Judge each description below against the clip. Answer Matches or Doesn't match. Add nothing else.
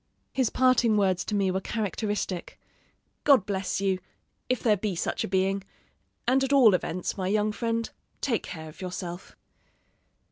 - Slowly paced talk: Doesn't match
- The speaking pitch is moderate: Doesn't match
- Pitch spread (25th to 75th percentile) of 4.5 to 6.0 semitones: Doesn't match